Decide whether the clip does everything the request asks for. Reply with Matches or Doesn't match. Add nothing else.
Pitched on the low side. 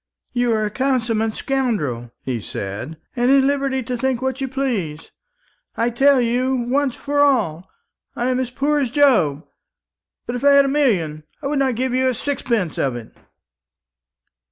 Doesn't match